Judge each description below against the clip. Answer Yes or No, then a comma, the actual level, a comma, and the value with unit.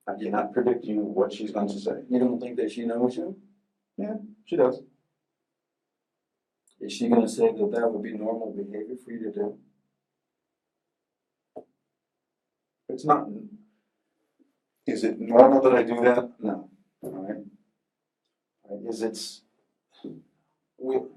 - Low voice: Yes, low, 125 Hz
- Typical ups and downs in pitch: No, wide, 7.4 semitones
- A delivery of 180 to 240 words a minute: No, average, 140 wpm